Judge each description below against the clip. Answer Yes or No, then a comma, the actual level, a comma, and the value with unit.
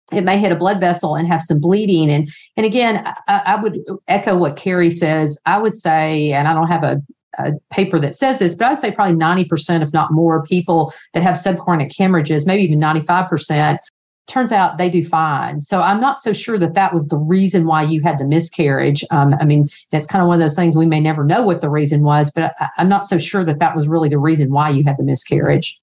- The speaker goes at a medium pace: No, fast, 250 wpm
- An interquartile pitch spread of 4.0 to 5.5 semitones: No, average, 3.5 semitones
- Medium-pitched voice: Yes, medium, 165 Hz